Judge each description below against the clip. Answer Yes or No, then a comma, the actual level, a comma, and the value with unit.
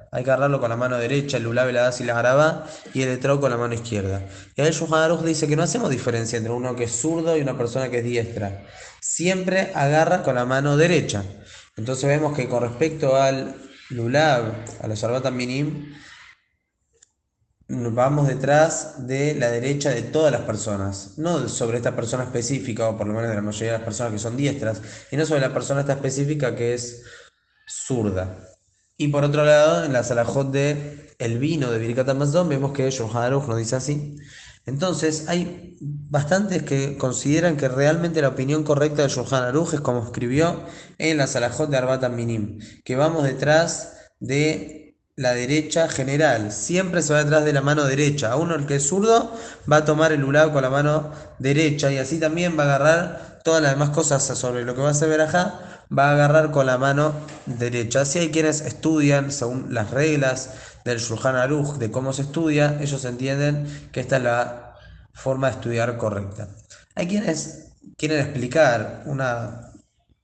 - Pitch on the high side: No, medium, 140 Hz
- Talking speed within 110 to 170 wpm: No, average, 185 wpm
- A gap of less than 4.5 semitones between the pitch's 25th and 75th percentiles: Yes, average, 4.1 semitones